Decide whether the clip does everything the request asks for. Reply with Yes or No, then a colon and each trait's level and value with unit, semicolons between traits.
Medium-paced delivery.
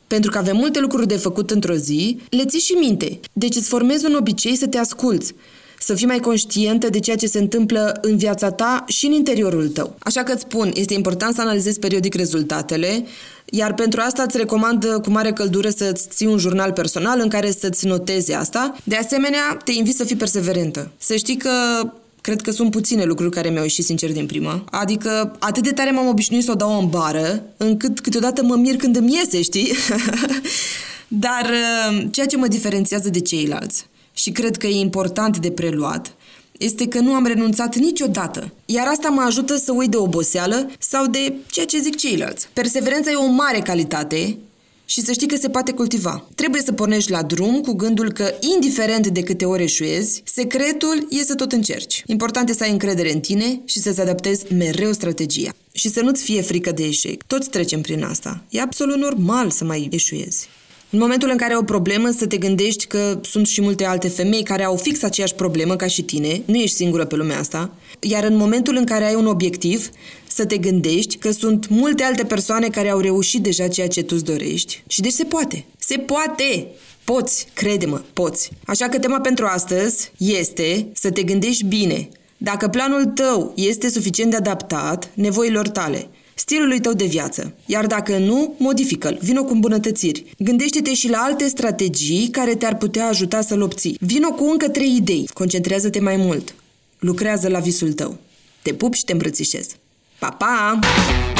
No: fast, 190 wpm